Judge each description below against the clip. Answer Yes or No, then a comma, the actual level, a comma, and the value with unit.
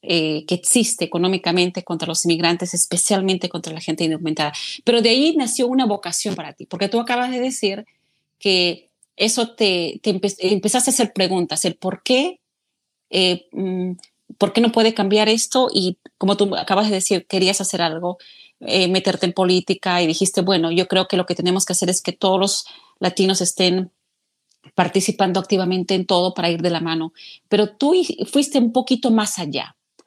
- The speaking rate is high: No, average, 180 wpm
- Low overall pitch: No, high, 190 Hz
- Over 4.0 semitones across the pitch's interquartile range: No, average, 3.0 semitones